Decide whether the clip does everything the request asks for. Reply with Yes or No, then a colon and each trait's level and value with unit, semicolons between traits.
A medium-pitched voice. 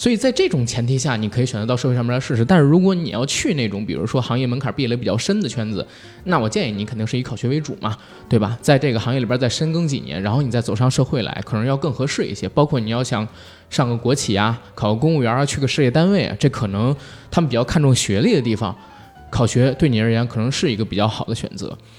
No: low, 125 Hz